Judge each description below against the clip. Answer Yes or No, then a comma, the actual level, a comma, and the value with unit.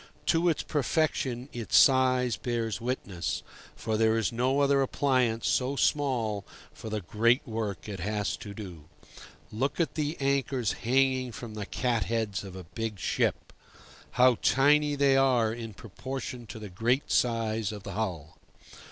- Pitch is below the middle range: Yes, low, 115 Hz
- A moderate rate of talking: Yes, average, 155 wpm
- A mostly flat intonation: No, average, 3.7 semitones